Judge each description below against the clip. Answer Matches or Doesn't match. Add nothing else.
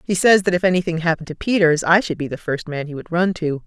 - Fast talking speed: Matches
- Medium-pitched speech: Matches